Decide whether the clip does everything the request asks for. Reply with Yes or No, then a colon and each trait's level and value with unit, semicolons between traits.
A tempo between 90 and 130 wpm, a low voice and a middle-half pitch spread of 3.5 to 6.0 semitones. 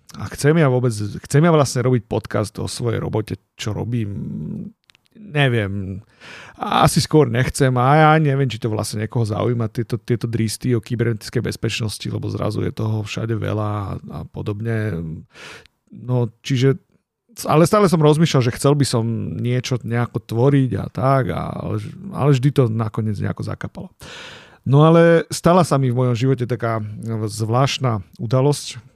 No: average, 155 wpm; low, 120 Hz; average, 4.1 semitones